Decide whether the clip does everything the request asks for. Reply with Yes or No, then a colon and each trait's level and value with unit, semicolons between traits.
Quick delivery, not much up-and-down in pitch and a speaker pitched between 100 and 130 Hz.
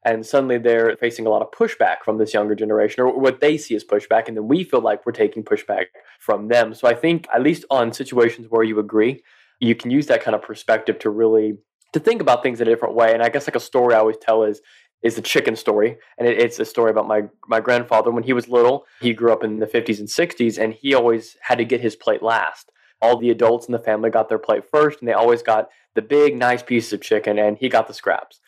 Yes: fast, 260 wpm; narrow, 1.9 semitones; low, 115 Hz